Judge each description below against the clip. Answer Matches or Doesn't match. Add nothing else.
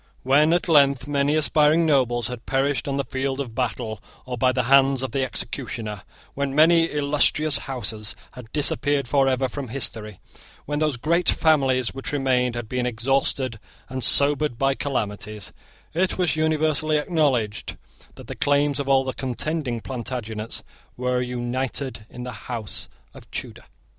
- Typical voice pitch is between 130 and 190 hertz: Matches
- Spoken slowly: Doesn't match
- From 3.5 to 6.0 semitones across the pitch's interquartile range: Doesn't match